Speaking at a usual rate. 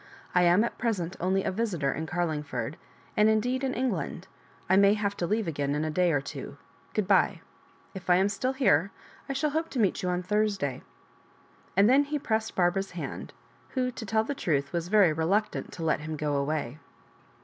No: fast, 210 wpm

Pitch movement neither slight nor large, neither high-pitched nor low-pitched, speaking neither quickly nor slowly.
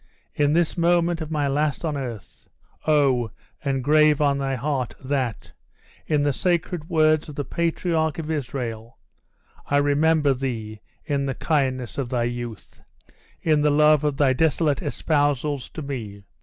Yes: average, 3.0 semitones; medium, 145 Hz; average, 150 wpm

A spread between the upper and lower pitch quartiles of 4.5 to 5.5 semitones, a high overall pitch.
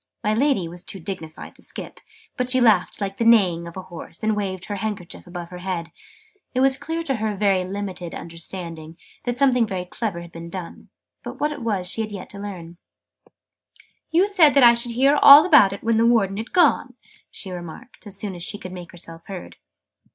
Yes: average, 5.0 semitones; high, 200 Hz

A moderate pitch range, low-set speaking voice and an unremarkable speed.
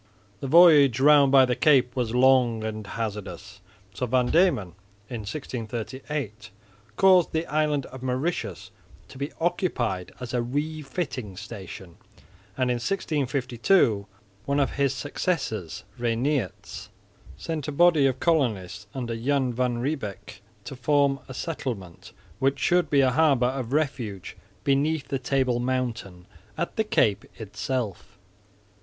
No: average, 4.2 semitones; low, 130 Hz; slow, 130 wpm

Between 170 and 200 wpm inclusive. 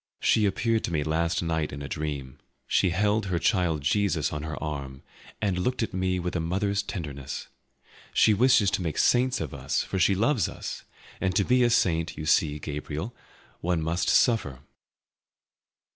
Yes: average, 175 wpm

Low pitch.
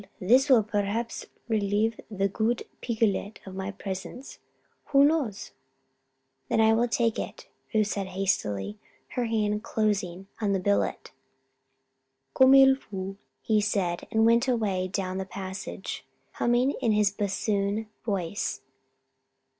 No: high, 210 Hz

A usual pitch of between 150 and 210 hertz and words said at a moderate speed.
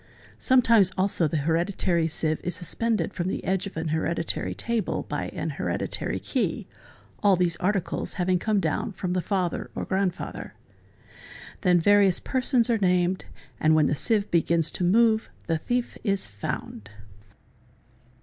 Yes: medium, 185 Hz; average, 150 wpm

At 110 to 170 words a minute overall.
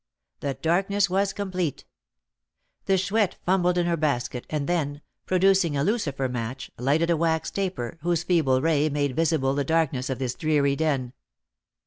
Yes: average, 155 wpm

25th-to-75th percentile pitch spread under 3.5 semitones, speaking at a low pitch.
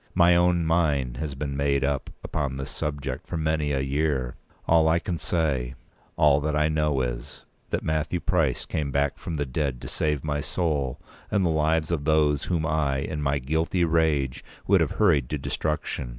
Yes: narrow, 2.5 semitones; very low, 75 Hz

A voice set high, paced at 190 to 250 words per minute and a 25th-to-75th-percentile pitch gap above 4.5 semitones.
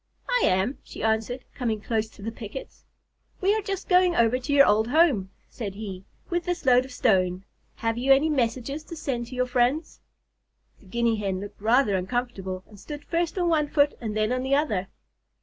Yes: high, 245 Hz; average, 195 wpm; average, 5.2 semitones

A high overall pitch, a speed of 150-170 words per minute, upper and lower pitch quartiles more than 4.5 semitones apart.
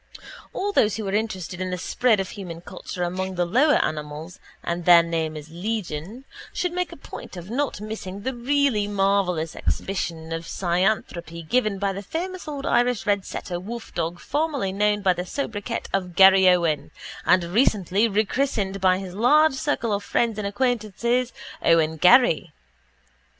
Yes: high, 195 Hz; average, 160 wpm; average, 5.1 semitones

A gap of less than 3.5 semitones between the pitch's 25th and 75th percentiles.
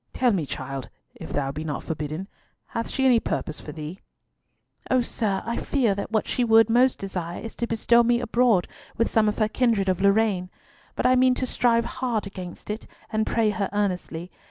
No: average, 4.5 semitones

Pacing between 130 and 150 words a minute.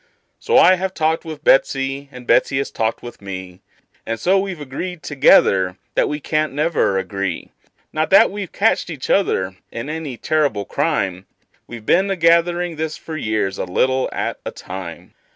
No: average, 170 wpm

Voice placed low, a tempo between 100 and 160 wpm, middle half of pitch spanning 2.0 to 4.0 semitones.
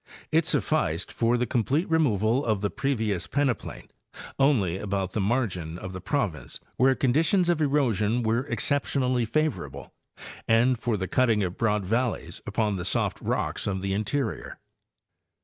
No: low, 115 Hz; average, 150 wpm; average, 5.3 semitones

